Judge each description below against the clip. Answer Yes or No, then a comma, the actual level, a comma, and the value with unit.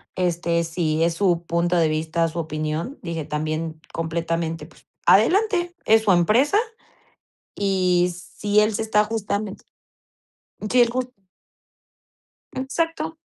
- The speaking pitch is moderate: Yes, medium, 175 Hz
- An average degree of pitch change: Yes, average, 5.0 semitones